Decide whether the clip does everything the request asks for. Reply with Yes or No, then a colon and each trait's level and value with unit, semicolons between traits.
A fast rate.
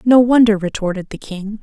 No: average, 185 wpm